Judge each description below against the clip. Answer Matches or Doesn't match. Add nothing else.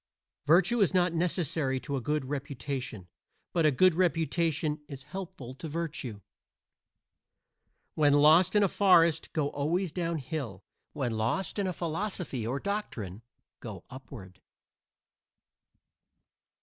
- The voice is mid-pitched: Matches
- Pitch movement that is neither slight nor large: Matches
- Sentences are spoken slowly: Matches